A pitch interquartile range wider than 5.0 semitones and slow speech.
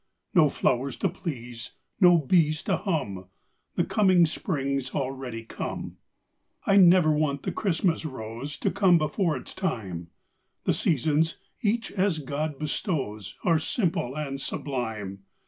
Yes: wide, 5.4 semitones; slow, 130 wpm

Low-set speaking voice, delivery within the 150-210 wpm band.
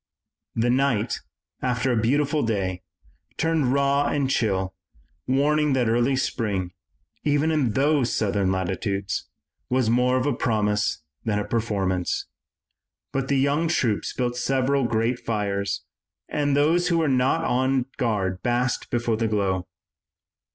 No: low, 125 Hz; slow, 135 wpm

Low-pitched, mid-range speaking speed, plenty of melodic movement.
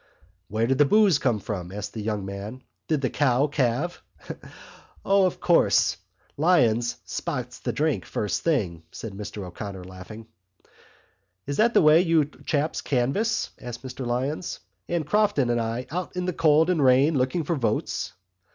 Yes: low, 130 Hz; average, 160 wpm; wide, 6.2 semitones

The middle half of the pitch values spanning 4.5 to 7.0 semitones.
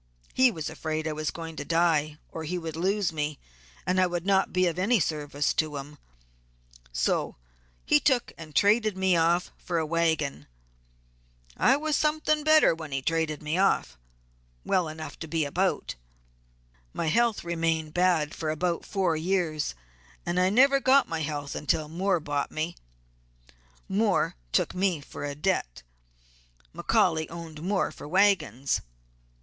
No: average, 3.6 semitones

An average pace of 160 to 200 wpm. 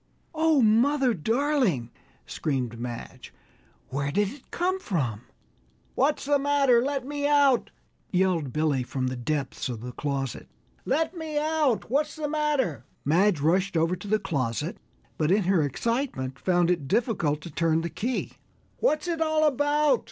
No: average, 150 wpm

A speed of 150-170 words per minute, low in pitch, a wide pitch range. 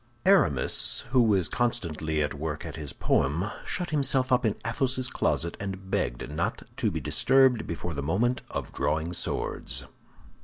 Yes: average, 155 wpm; very low, 95 Hz; wide, 8.4 semitones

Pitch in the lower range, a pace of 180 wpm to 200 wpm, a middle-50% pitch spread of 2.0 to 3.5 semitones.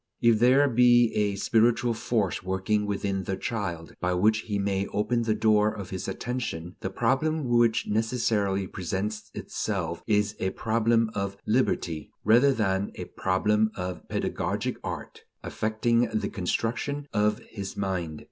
No: low, 105 Hz; average, 145 wpm; average, 3.2 semitones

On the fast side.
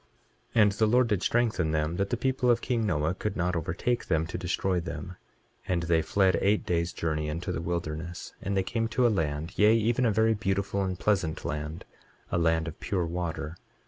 Yes: fast, 215 wpm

